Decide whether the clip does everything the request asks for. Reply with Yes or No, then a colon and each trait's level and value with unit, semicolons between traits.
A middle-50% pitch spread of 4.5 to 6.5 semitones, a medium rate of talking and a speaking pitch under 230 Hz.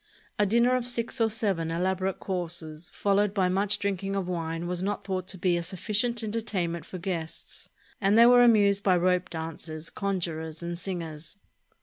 No: average, 3.2 semitones; average, 170 wpm; medium, 185 Hz